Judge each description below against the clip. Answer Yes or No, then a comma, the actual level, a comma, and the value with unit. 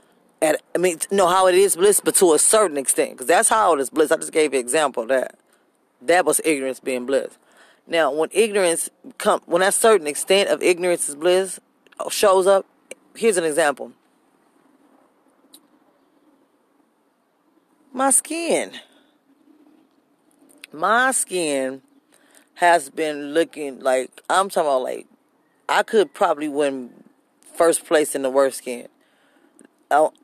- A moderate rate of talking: Yes, average, 145 wpm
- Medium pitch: No, high, 210 Hz